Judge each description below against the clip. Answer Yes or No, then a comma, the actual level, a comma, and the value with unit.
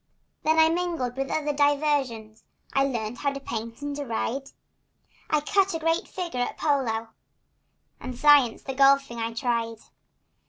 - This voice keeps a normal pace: Yes, average, 155 wpm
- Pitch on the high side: Yes, very high, 275 Hz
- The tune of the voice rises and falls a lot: No, average, 4.1 semitones